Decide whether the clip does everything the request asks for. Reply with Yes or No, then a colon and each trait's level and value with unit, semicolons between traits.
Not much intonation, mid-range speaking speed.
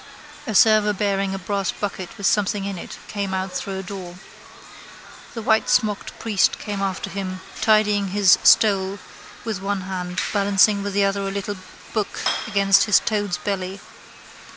Yes: narrow, 1.4 semitones; average, 155 wpm